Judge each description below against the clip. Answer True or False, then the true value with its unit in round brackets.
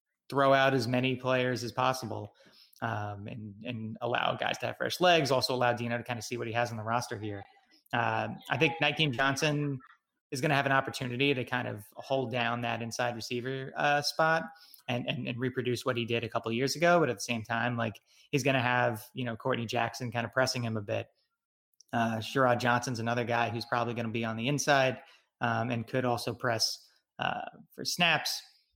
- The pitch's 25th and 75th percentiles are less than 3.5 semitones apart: True (2.5 semitones)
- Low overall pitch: True (120 Hz)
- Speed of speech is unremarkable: False (215 wpm)